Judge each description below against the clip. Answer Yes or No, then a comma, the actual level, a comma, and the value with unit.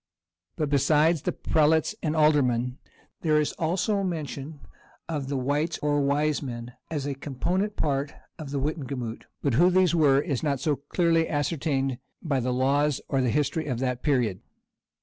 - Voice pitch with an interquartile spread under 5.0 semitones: Yes, average, 2.8 semitones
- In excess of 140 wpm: Yes, average, 160 wpm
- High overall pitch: No, medium, 145 Hz